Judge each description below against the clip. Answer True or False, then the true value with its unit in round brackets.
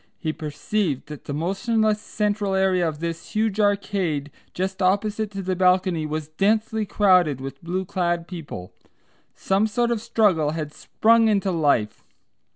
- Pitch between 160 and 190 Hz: True (185 Hz)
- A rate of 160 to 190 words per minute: False (150 wpm)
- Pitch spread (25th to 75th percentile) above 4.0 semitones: True (4.9 semitones)